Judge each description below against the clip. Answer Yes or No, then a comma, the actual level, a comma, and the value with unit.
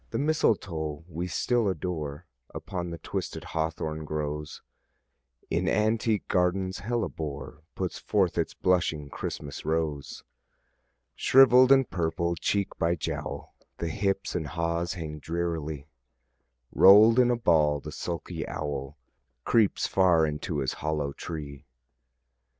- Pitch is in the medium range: No, very low, 85 Hz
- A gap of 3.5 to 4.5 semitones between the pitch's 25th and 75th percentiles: Yes, average, 4.2 semitones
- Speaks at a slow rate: Yes, slow, 120 wpm